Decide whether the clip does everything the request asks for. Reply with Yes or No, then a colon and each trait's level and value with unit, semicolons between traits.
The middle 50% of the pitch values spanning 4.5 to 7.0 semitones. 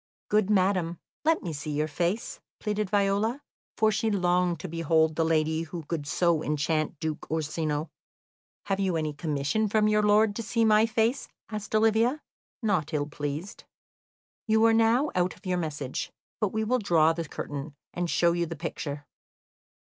Yes: average, 5.3 semitones